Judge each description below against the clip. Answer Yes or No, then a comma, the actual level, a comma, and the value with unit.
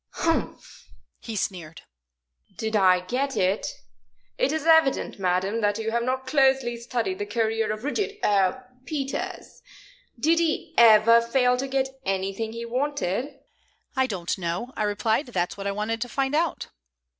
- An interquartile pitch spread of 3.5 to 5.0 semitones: Yes, average, 4.6 semitones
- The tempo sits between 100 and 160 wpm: Yes, average, 155 wpm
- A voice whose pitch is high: Yes, high, 230 Hz